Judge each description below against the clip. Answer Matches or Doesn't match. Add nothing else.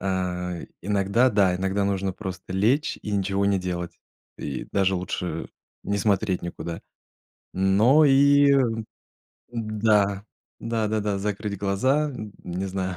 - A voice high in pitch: Doesn't match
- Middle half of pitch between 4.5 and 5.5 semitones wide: Doesn't match